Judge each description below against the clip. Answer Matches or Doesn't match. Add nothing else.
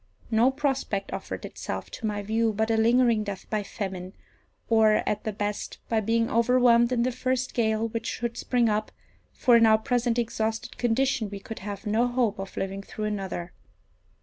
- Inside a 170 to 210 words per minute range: Matches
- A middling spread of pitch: Doesn't match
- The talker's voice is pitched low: Doesn't match